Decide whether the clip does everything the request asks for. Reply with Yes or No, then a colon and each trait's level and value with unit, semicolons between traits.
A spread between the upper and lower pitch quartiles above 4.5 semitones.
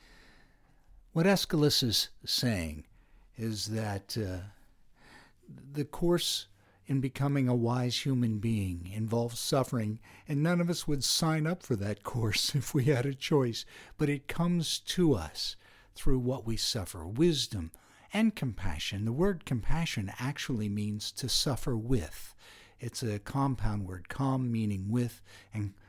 Yes: wide, 5.6 semitones